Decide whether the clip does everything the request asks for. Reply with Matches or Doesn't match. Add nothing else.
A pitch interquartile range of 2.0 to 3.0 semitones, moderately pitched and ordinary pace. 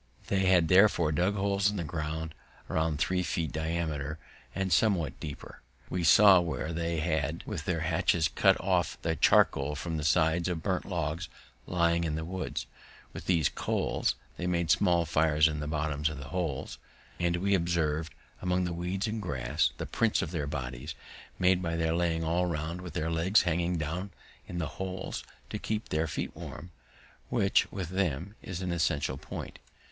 Doesn't match